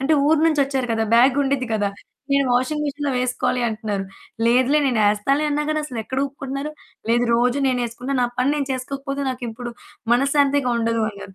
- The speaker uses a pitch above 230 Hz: Yes, very high, 260 Hz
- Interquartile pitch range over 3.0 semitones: No, average, 2.7 semitones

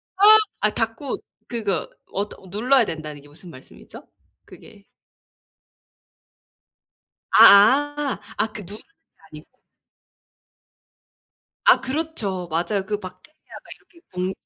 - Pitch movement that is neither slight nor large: No, wide, 6.4 semitones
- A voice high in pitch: Yes, high, 210 Hz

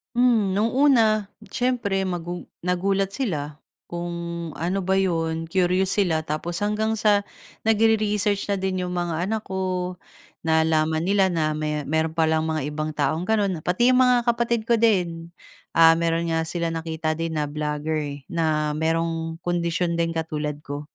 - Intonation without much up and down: No, average, 3.7 semitones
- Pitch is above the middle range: No, medium, 170 Hz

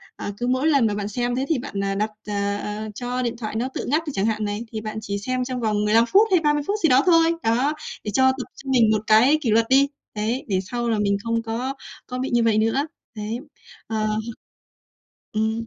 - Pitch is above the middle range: Yes, high, 230 Hz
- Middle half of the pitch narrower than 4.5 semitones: Yes, average, 3.5 semitones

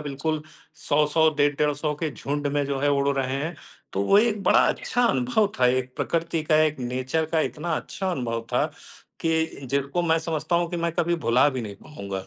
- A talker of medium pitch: Yes, medium, 150 Hz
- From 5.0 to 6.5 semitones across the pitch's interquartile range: No, average, 3.6 semitones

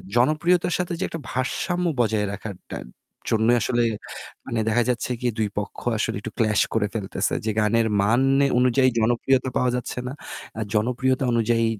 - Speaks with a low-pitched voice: Yes, low, 120 Hz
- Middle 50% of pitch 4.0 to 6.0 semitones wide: No, average, 2.8 semitones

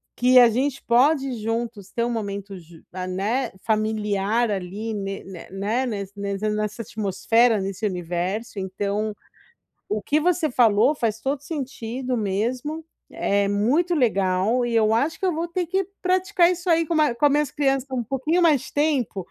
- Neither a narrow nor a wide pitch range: No, wide, 5.7 semitones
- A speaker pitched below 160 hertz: No, high, 230 Hz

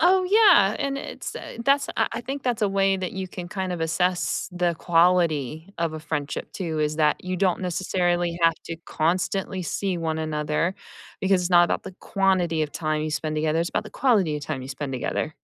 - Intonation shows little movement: No, average, 3.5 semitones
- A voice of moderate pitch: Yes, medium, 175 Hz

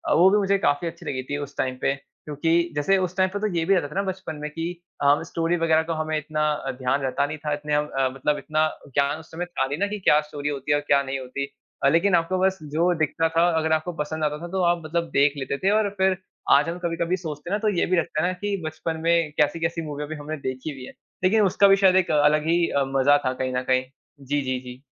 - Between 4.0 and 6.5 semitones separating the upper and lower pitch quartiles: No, average, 3.2 semitones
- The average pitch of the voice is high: No, medium, 155 Hz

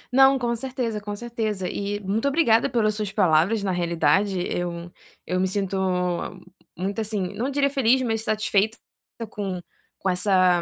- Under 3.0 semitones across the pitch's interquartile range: No, average, 3.5 semitones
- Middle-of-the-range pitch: No, high, 205 Hz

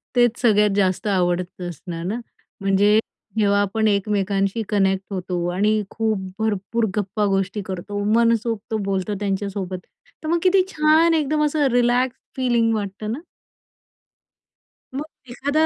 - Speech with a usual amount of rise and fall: Yes, average, 3.5 semitones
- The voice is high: Yes, high, 210 Hz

